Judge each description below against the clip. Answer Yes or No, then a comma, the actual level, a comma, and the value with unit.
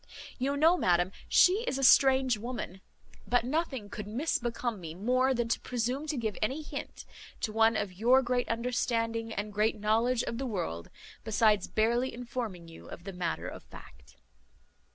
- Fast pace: No, average, 170 wpm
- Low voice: No, high, 230 Hz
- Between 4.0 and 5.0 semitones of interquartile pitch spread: No, average, 3.4 semitones